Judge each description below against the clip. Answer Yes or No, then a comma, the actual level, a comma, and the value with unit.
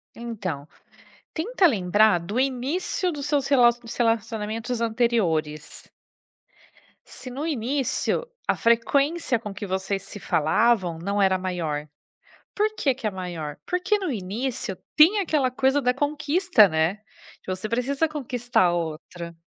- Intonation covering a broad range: Yes, wide, 6.6 semitones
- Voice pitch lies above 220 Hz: Yes, high, 230 Hz